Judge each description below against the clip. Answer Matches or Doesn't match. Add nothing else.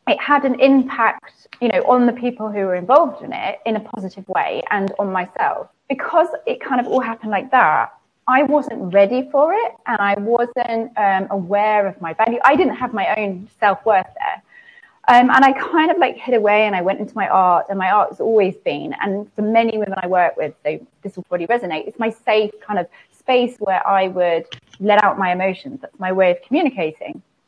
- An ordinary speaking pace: Doesn't match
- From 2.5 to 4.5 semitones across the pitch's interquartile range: Doesn't match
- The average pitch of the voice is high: Matches